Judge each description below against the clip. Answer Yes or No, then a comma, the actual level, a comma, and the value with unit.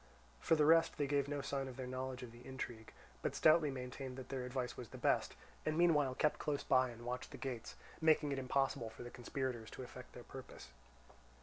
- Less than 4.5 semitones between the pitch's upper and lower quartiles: Yes, narrow, 2.4 semitones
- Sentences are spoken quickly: Yes, fast, 215 wpm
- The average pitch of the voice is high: No, low, 130 Hz